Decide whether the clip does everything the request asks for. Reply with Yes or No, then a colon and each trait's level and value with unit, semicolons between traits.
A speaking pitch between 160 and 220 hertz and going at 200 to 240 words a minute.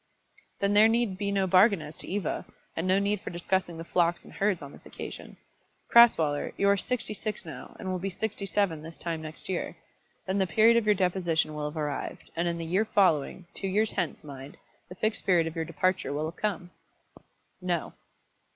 Yes: medium, 185 Hz; fast, 205 wpm